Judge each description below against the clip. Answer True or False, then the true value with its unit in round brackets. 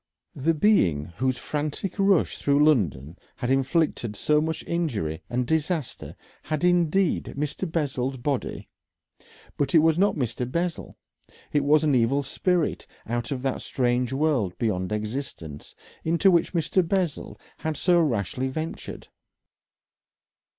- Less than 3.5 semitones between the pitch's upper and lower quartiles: False (5.0 semitones)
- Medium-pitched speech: True (145 Hz)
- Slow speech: True (130 wpm)